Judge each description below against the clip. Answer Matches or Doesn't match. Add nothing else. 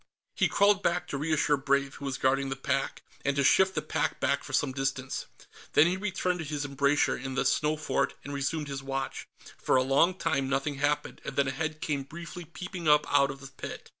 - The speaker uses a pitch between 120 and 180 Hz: Matches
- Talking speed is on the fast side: Matches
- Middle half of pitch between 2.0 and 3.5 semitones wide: Matches